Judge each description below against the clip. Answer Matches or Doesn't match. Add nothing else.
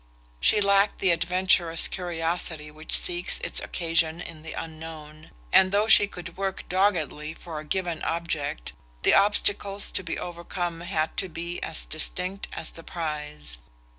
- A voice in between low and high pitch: Matches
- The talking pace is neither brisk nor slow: Matches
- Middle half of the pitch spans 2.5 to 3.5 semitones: Matches